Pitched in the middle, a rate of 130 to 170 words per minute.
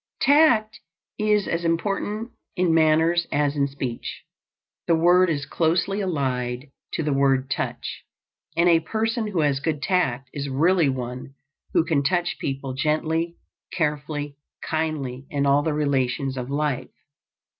Yes: medium, 150 Hz; average, 140 wpm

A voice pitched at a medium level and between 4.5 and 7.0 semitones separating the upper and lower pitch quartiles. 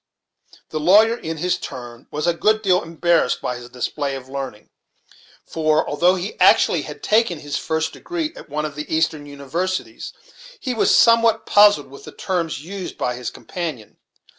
Yes: medium, 160 Hz; average, 4.9 semitones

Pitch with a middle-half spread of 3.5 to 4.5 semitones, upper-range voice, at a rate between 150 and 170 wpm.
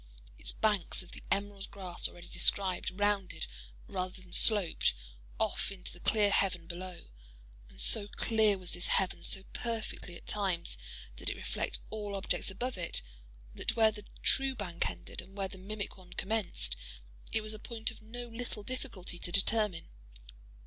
No: average, 3.0 semitones; high, 195 Hz; average, 165 wpm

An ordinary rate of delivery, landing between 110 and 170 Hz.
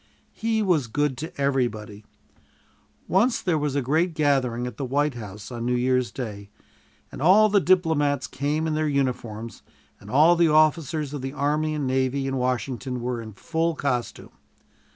Yes: average, 170 wpm; medium, 140 Hz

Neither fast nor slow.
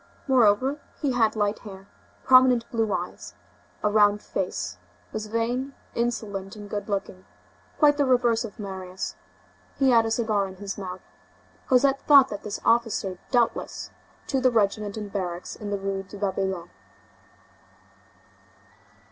Yes: average, 145 wpm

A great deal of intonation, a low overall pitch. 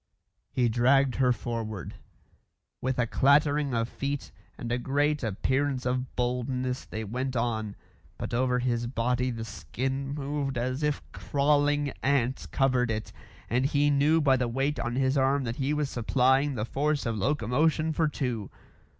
No: average, 2.9 semitones; low, 130 Hz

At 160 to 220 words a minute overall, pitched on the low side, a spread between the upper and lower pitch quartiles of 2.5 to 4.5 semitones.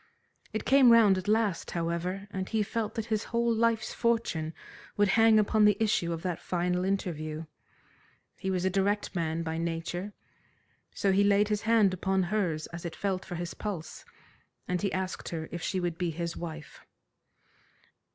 No: average, 175 wpm; high, 190 Hz; average, 3.7 semitones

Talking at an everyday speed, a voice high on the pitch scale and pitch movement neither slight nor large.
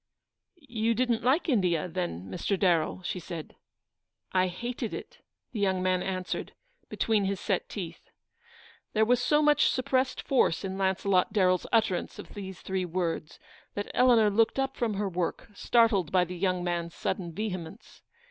Yes: average, 165 wpm; high, 195 Hz; average, 4.4 semitones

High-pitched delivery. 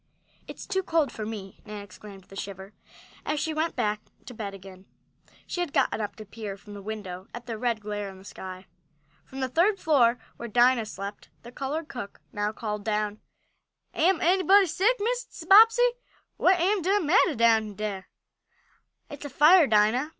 Yes: high, 230 Hz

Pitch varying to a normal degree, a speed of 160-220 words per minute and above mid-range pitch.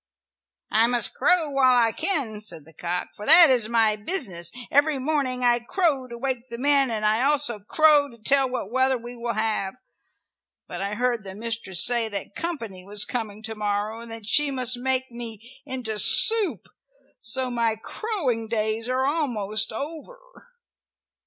Yes: average, 3.8 semitones; average, 170 wpm; high, 235 Hz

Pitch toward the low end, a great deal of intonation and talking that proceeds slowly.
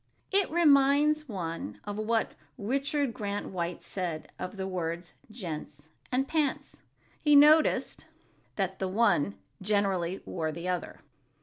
No: high, 200 Hz; wide, 8.0 semitones; slow, 120 wpm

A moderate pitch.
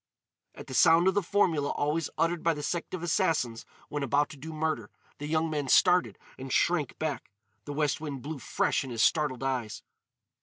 Yes: medium, 150 Hz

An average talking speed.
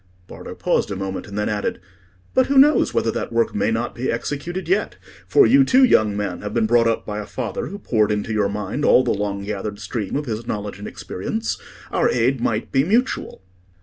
No: fast, 215 wpm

